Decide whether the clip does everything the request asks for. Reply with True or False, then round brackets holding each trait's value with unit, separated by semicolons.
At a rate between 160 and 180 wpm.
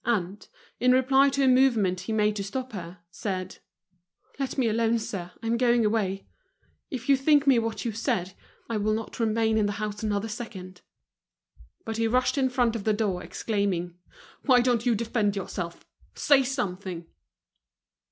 True (170 wpm)